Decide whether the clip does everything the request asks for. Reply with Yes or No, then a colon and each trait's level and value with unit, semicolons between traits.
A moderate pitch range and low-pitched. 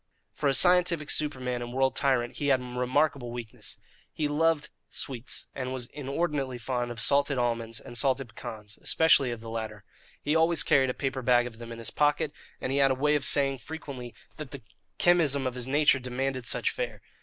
Yes: average, 3.2 semitones; low, 130 Hz